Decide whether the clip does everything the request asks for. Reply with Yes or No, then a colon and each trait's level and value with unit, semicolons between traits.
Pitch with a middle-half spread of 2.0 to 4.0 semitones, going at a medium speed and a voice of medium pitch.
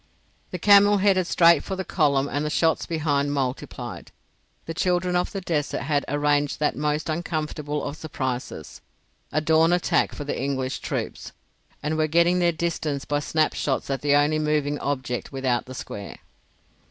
Yes: average, 2.9 semitones; average, 165 wpm; medium, 150 Hz